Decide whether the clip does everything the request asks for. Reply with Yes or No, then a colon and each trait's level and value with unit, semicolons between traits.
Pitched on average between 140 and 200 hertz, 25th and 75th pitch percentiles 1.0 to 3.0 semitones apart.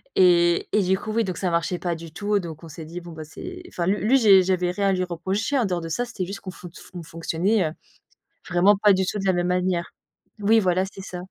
Yes: medium, 185 Hz; narrow, 2.6 semitones